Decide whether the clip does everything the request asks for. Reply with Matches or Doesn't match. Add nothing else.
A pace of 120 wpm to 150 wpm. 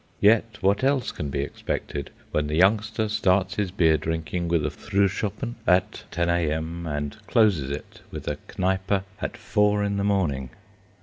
Doesn't match